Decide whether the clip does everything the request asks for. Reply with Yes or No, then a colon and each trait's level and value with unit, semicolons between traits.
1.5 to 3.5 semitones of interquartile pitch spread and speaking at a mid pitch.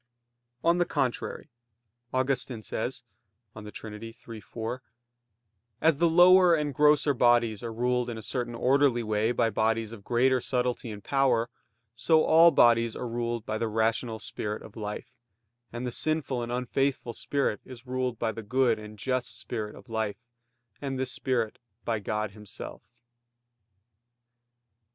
No: average, 2.8 semitones; low, 120 Hz